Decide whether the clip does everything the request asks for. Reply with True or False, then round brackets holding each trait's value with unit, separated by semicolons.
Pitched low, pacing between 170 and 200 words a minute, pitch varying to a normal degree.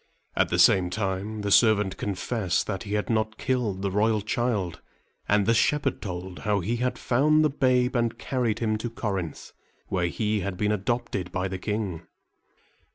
True (105 Hz; 175 wpm; 3.6 semitones)